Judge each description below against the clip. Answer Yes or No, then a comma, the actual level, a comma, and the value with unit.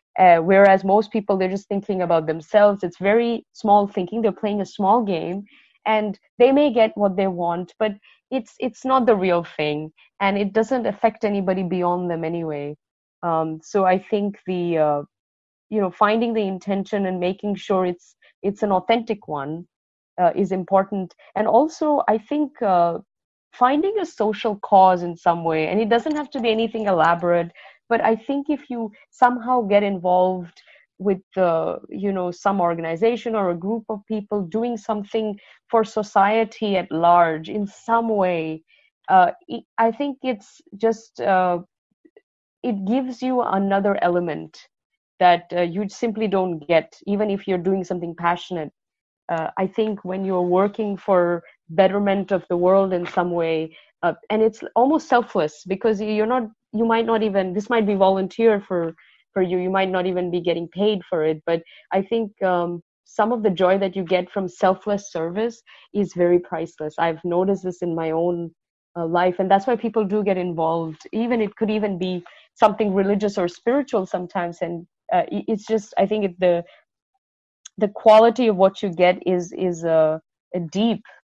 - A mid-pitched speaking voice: No, high, 195 Hz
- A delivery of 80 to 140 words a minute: No, average, 175 wpm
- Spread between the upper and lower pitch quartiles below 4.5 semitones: Yes, average, 3.8 semitones